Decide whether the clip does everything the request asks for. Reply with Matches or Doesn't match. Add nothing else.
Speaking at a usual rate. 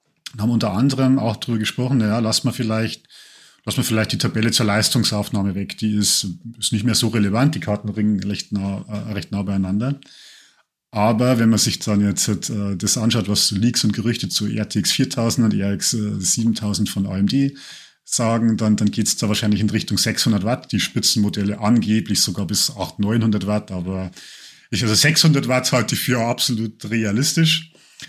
Matches